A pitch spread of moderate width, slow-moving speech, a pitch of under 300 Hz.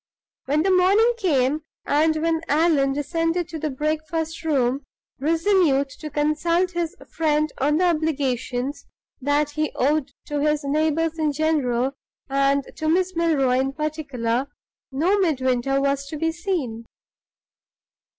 No: average, 3.0 semitones; slow, 130 wpm; very high, 305 Hz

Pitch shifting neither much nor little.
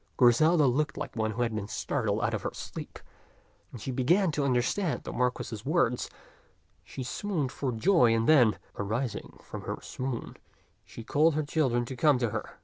Yes: average, 4.5 semitones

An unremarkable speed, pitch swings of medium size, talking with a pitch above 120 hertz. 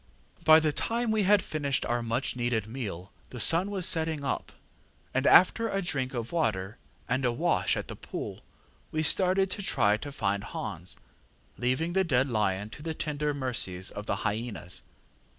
No: average, 175 wpm; wide, 6.6 semitones; low, 135 Hz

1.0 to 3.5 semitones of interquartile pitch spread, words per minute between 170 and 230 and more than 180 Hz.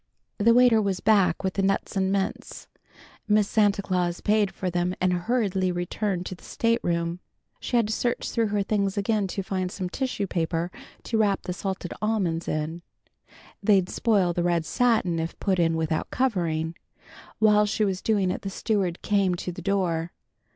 Yes: average, 3.1 semitones; average, 180 wpm; high, 190 Hz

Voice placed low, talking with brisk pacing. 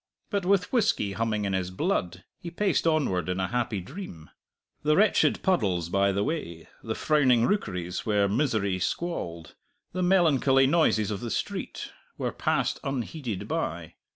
No: low, 115 Hz; average, 155 wpm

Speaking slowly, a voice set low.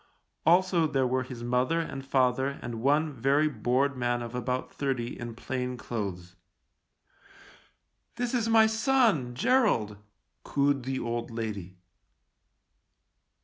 Yes: slow, 125 wpm; low, 130 Hz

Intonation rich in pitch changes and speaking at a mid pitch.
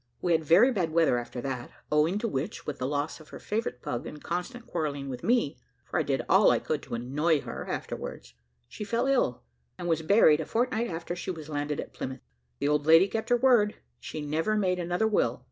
Yes: wide, 6.3 semitones; medium, 165 Hz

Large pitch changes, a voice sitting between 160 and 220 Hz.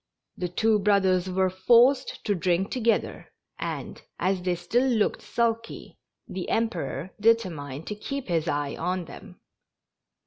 No: average, 4.4 semitones; high, 190 Hz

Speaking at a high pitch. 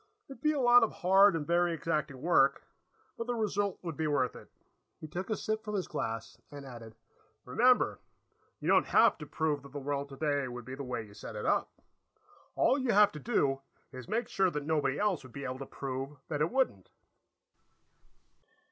No: medium, 150 Hz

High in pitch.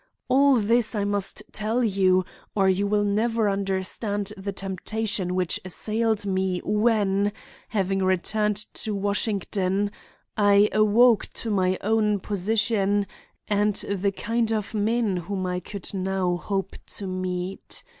Yes: high, 205 Hz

